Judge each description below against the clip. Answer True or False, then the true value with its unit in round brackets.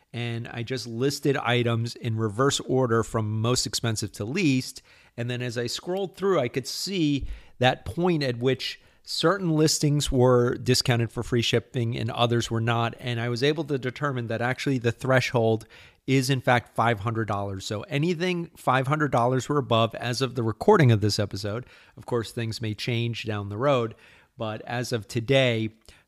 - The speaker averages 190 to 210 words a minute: False (175 wpm)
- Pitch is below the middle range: True (120 Hz)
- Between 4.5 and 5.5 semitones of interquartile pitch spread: False (2.9 semitones)